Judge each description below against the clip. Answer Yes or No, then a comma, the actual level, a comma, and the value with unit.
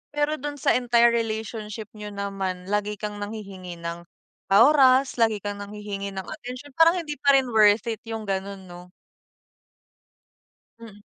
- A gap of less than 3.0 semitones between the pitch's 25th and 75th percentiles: No, average, 3.8 semitones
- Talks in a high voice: Yes, high, 210 Hz